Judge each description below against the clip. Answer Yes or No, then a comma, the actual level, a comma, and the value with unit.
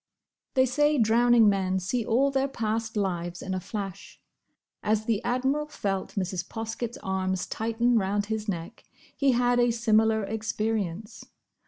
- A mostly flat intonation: No, average, 3.6 semitones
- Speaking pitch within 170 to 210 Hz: No, high, 220 Hz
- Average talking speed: Yes, average, 145 wpm